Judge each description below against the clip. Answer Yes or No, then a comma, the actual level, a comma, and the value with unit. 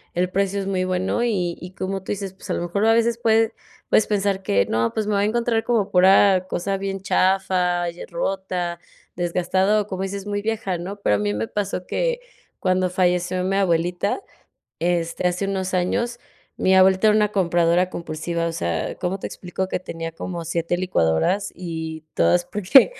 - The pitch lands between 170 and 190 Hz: Yes, medium, 185 Hz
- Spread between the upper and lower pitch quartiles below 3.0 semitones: Yes, narrow, 2.4 semitones